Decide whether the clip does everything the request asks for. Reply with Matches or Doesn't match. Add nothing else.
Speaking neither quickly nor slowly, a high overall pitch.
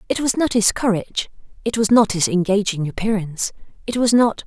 Matches